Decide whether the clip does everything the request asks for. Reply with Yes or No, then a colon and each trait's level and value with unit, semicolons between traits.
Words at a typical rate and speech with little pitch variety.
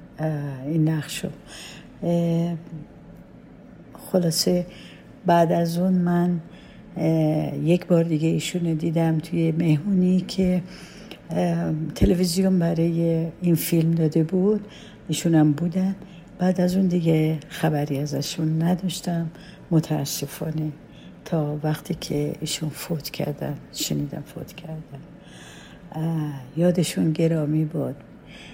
No: slow, 95 wpm; narrow, 2.3 semitones